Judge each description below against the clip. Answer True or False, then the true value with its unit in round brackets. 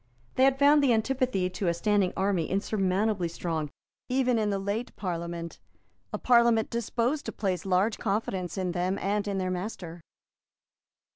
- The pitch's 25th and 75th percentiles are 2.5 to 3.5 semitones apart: False (4.1 semitones)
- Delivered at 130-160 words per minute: True (155 wpm)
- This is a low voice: False (200 Hz)